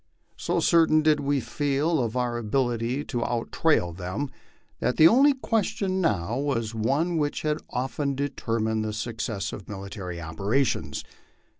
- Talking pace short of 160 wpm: Yes, average, 150 wpm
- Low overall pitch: Yes, low, 125 Hz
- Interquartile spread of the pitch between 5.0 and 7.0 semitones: Yes, average, 5.3 semitones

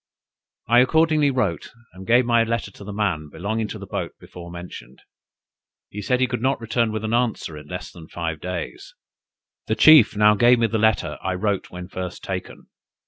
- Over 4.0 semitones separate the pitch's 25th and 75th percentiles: Yes, average, 4.8 semitones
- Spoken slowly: No, average, 195 wpm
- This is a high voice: No, low, 105 Hz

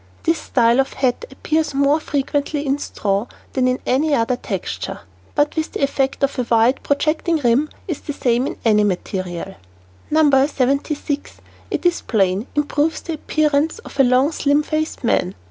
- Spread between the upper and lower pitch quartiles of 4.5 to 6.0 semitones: No, average, 3.6 semitones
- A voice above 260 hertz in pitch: Yes, very high, 280 Hz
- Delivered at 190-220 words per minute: No, average, 165 wpm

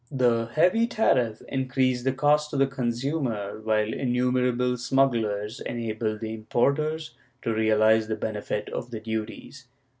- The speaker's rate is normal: No, slow, 130 wpm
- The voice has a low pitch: Yes, low, 120 Hz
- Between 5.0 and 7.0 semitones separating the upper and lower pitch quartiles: No, average, 3.4 semitones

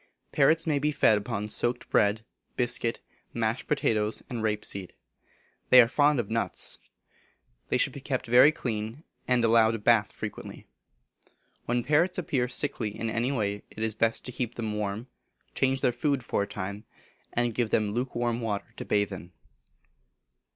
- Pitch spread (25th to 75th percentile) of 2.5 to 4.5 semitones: Yes, average, 3.0 semitones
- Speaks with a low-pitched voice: Yes, low, 115 Hz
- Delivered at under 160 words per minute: No, average, 165 wpm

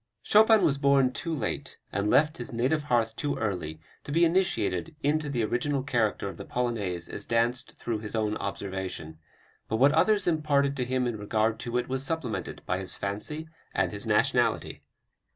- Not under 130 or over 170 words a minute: No, average, 180 wpm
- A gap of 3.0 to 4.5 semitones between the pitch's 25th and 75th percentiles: No, wide, 5.4 semitones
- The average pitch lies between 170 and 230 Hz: No, low, 125 Hz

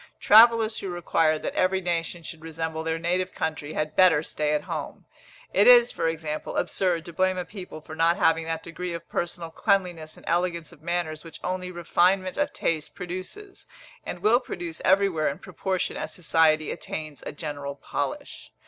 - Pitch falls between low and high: Yes, medium, 170 Hz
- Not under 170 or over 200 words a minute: Yes, average, 175 wpm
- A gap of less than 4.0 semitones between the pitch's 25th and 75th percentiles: Yes, narrow, 2.6 semitones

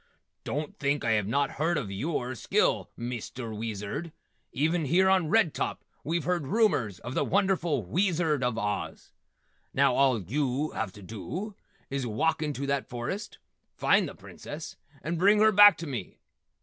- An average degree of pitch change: No, wide, 6.3 semitones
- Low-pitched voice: No, medium, 145 Hz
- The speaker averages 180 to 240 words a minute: No, average, 160 wpm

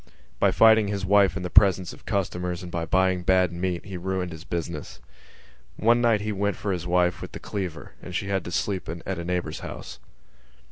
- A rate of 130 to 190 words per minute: No, fast, 205 wpm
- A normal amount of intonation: No, narrow, 2.1 semitones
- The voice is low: Yes, very low, 95 Hz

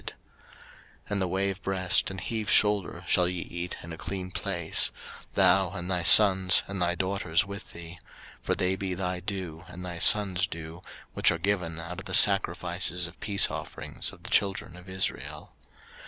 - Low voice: Yes, very low, 90 Hz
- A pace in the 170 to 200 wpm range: Yes, average, 180 wpm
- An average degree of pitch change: No, narrow, 2.0 semitones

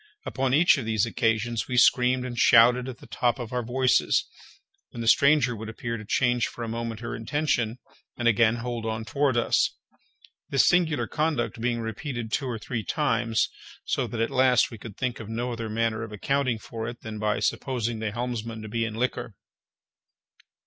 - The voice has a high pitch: No, low, 120 Hz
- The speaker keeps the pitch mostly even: Yes, narrow, 2.0 semitones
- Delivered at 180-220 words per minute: Yes, average, 190 wpm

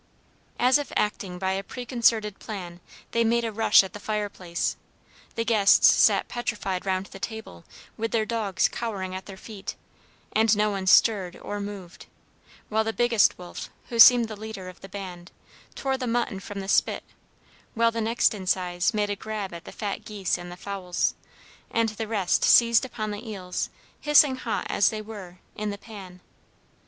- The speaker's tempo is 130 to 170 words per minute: No, average, 180 wpm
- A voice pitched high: Yes, high, 210 Hz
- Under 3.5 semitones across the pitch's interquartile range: Yes, average, 3.1 semitones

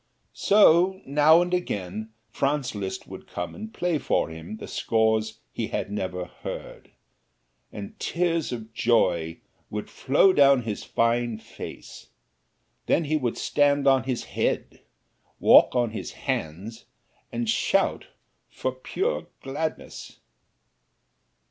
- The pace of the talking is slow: Yes, slow, 125 wpm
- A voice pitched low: Yes, low, 120 Hz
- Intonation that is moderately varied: No, wide, 5.7 semitones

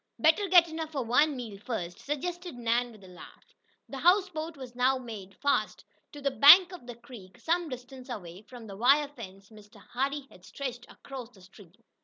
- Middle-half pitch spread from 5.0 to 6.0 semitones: Yes, average, 5.3 semitones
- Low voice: No, very high, 250 Hz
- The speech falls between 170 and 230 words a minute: Yes, average, 190 wpm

